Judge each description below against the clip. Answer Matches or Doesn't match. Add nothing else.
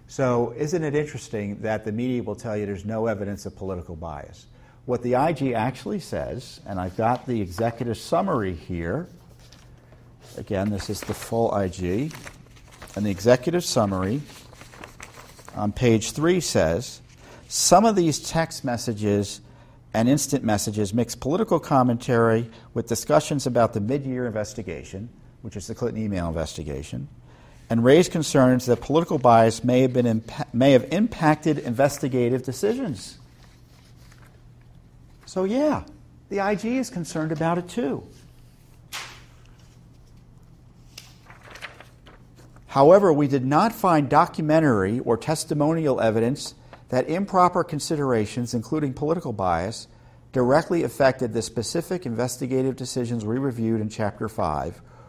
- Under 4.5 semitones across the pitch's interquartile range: Doesn't match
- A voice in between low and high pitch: Doesn't match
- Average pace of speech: Doesn't match